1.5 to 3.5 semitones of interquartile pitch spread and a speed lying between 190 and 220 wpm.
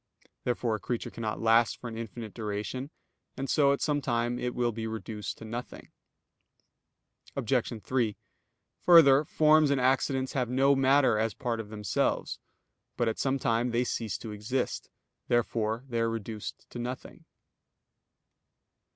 No: average, 2.9 semitones; average, 150 wpm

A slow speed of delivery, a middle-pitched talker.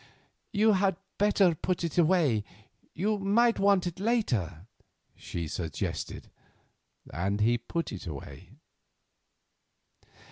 Yes: slow, 105 wpm; medium, 170 Hz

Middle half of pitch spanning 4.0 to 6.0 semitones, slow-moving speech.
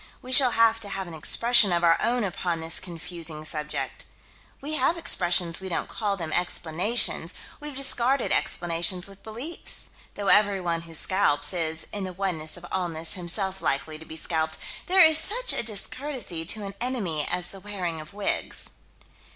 No: wide, 5.5 semitones; average, 170 wpm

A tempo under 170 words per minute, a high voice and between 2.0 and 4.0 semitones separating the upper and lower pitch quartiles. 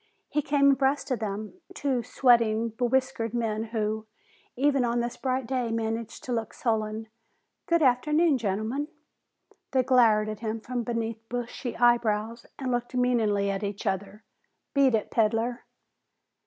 Yes: average, 140 wpm; high, 235 Hz; average, 2.8 semitones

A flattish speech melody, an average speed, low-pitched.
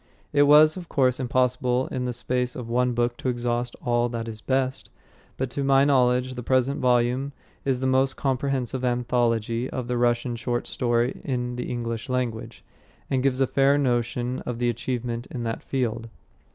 Yes: narrow, 1.5 semitones; average, 180 wpm; low, 125 Hz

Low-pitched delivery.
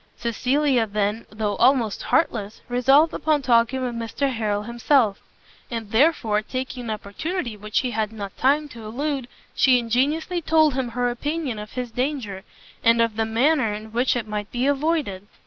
No: high, 240 Hz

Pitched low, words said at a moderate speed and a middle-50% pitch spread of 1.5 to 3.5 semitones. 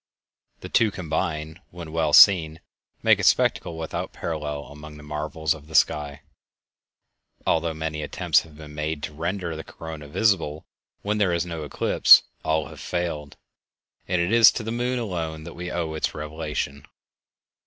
Yes: very low, 80 Hz; average, 165 wpm; narrow, 2.4 semitones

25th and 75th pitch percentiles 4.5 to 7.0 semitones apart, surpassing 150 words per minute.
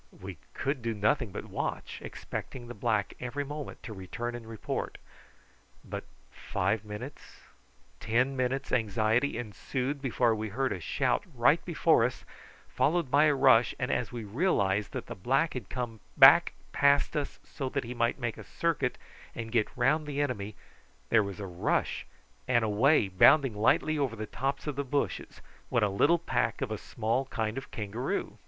No: average, 4.1 semitones; average, 175 wpm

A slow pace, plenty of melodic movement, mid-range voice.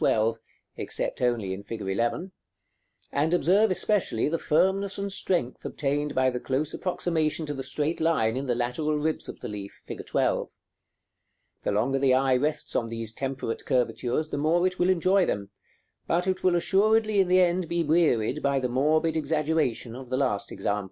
No: average, 180 wpm; wide, 5.9 semitones; medium, 150 Hz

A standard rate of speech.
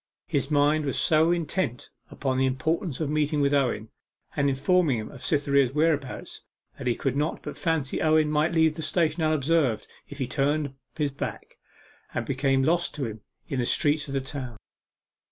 Yes: average, 180 wpm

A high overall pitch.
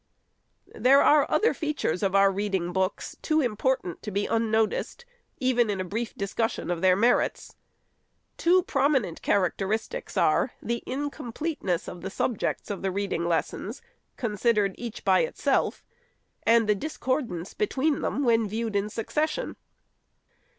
Yes: high, 225 Hz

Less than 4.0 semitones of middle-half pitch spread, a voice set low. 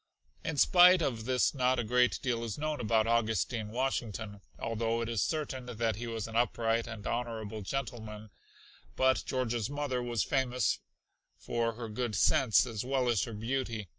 Yes: narrow, 2.5 semitones; low, 120 Hz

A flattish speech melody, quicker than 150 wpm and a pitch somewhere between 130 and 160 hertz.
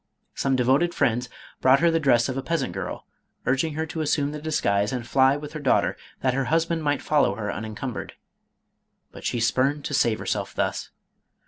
No: average, 3.6 semitones; average, 200 wpm; low, 135 Hz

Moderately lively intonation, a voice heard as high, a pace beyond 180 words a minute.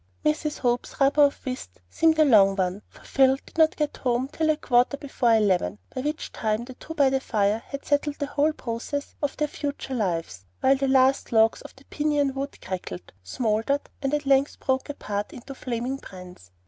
Yes: average, 4.6 semitones; very high, 265 Hz; average, 200 wpm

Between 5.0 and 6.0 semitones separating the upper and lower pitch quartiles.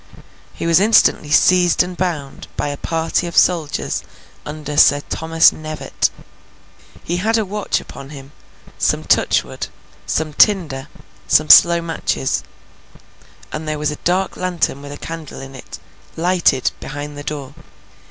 No: average, 3.3 semitones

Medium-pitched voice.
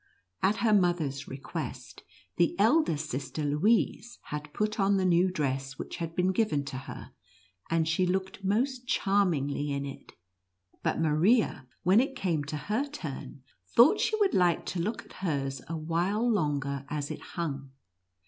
Yes: medium, 170 Hz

